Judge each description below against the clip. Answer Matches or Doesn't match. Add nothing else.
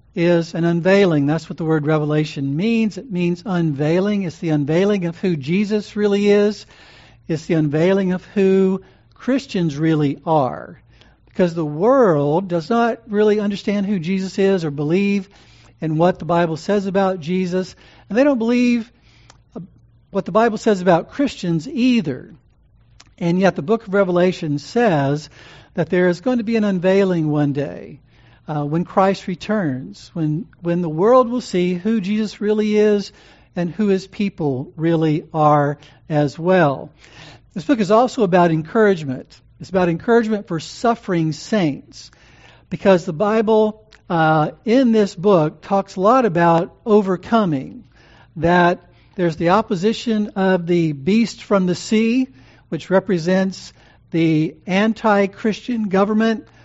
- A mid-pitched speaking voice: Matches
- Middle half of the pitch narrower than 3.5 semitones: Doesn't match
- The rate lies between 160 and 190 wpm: Doesn't match